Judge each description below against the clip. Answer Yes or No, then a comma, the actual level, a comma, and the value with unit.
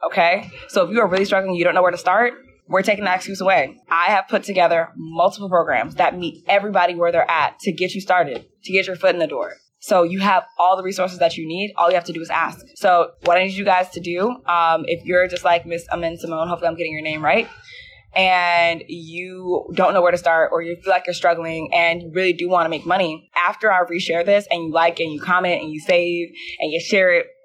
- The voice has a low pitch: No, medium, 180 Hz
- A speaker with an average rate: No, fast, 255 wpm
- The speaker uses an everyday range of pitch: No, narrow, 2.1 semitones